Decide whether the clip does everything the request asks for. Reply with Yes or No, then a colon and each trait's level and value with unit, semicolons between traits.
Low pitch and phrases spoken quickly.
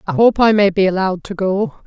No: high, 195 Hz; fast, 255 wpm